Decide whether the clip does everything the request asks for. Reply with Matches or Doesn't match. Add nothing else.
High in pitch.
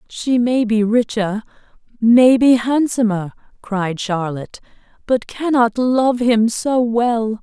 Matches